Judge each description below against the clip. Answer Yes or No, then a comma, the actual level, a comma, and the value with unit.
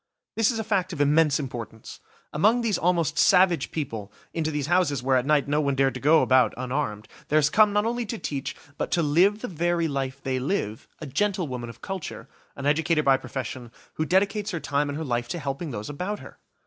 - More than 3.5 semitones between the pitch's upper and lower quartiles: Yes, average, 5.2 semitones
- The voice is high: No, medium, 150 Hz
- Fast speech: Yes, fast, 215 wpm